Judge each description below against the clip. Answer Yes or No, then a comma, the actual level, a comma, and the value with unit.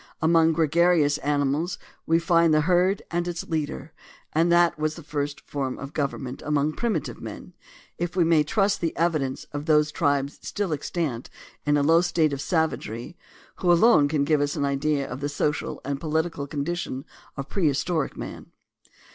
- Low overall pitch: No, medium, 155 Hz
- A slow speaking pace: No, average, 170 wpm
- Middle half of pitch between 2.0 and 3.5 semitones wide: Yes, average, 2.9 semitones